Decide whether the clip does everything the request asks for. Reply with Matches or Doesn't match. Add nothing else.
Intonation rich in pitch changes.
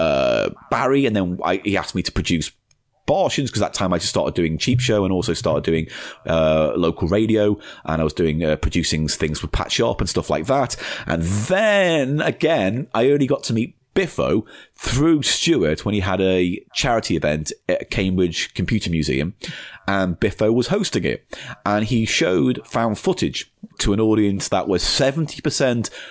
Matches